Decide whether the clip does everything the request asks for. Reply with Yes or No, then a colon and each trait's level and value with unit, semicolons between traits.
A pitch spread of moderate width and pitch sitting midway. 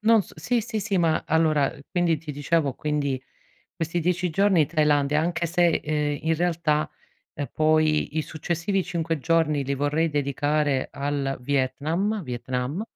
Yes: average, 3.0 semitones; medium, 155 Hz